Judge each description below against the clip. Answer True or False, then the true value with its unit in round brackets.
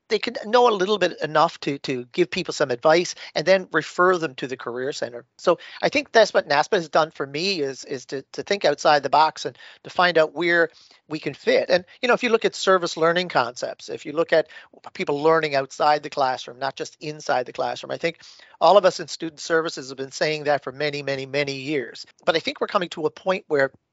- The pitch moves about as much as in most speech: True (3.8 semitones)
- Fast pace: True (245 wpm)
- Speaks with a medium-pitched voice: True (160 Hz)